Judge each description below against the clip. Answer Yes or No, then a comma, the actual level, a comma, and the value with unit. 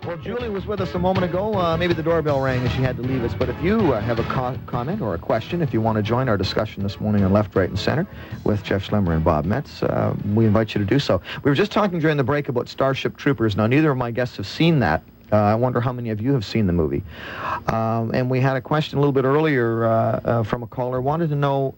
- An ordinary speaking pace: No, fast, 285 wpm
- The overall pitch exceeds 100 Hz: Yes, low, 125 Hz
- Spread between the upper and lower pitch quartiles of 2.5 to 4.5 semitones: No, average, 5.0 semitones